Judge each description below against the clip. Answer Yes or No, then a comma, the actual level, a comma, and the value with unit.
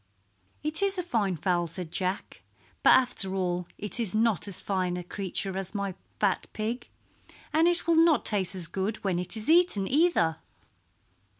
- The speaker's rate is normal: Yes, average, 175 wpm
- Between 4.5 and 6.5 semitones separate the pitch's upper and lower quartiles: Yes, average, 5.3 semitones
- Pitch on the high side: Yes, high, 200 Hz